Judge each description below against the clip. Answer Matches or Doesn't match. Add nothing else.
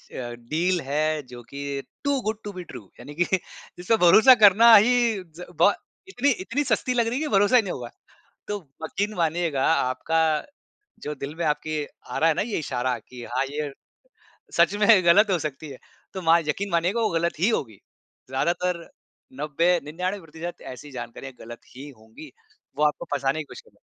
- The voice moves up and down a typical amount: Doesn't match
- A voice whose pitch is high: Doesn't match